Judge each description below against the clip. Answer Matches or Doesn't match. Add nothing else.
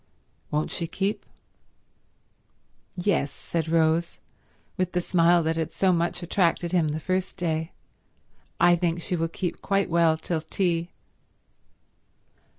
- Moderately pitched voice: Matches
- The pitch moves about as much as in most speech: Doesn't match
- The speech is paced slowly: Matches